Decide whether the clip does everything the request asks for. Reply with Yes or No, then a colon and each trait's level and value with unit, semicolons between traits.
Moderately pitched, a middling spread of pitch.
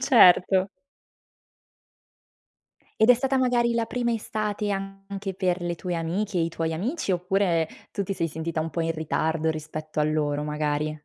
Yes: medium, 180 Hz; average, 4.4 semitones